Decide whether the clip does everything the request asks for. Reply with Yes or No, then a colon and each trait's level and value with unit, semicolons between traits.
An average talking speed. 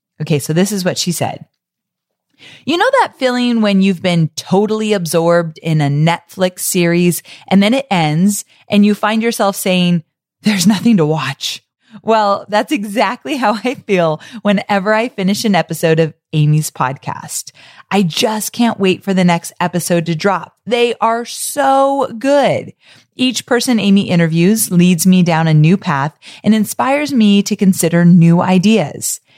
Yes: average, 160 wpm